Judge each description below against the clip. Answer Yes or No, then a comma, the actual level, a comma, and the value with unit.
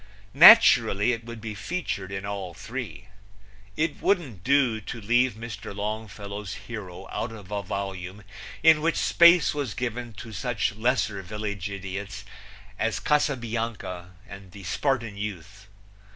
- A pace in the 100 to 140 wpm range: Yes, slow, 135 wpm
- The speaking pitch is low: Yes, low, 110 Hz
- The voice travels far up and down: No, average, 3.8 semitones